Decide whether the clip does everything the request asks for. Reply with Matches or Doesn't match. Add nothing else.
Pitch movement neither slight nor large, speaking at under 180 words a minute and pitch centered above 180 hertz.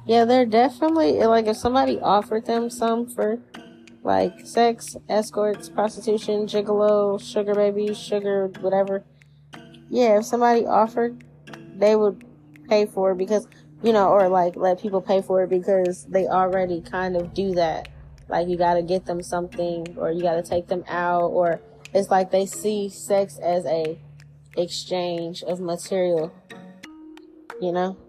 Matches